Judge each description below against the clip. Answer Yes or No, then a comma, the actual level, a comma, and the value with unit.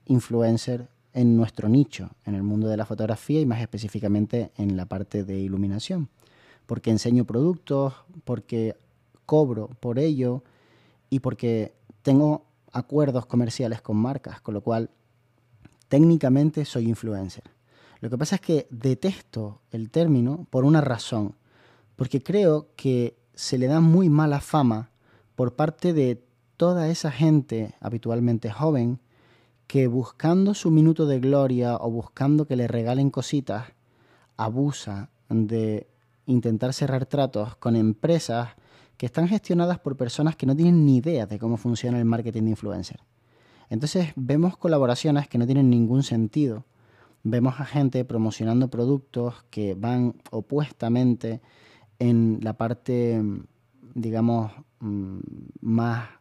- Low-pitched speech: Yes, low, 120 Hz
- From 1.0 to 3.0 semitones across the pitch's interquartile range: No, average, 3.5 semitones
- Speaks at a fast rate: No, average, 130 wpm